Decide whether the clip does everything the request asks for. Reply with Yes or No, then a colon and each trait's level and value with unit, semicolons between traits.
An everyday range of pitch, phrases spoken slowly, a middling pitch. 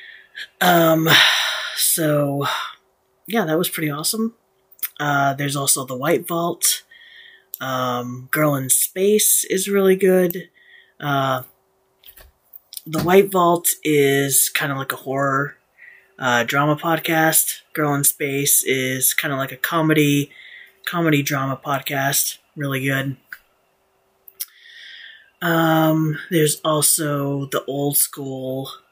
Yes: average, 3.7 semitones; slow, 110 wpm; medium, 150 Hz